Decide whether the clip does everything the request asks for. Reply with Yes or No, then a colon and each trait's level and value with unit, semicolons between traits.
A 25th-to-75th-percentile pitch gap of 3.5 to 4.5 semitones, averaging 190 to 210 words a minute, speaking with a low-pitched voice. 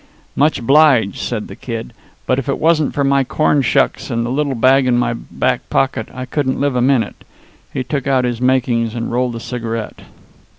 No: average, 2.7 semitones; average, 200 wpm; low, 130 Hz